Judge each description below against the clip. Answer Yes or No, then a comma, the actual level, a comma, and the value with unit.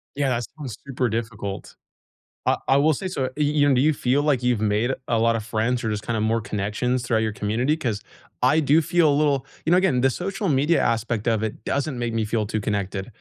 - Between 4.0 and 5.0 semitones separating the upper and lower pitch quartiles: Yes, average, 4.6 semitones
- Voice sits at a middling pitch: No, low, 125 Hz